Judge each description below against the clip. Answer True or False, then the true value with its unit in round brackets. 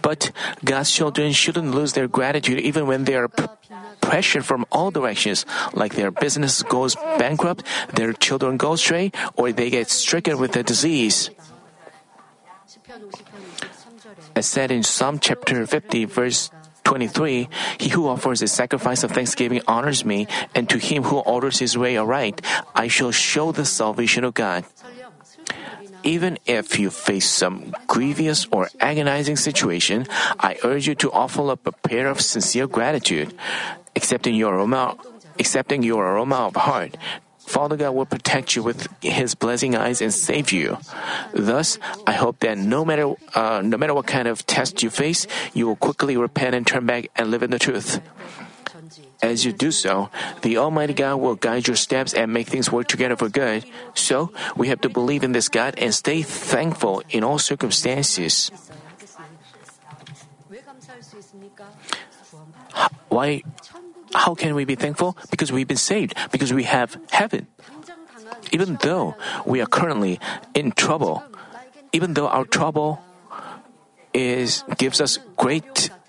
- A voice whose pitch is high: False (145 Hz)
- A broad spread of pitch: False (4.6 semitones)